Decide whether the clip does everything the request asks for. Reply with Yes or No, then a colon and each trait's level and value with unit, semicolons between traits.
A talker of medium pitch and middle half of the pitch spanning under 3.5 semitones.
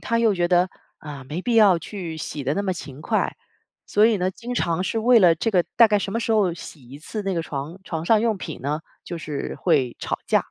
No: medium, 180 Hz; wide, 5.4 semitones